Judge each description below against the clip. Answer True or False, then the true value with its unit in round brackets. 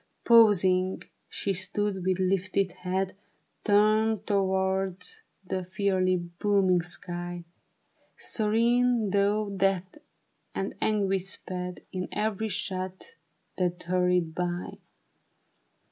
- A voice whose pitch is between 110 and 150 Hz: False (190 Hz)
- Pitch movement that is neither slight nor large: False (2.2 semitones)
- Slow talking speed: True (90 wpm)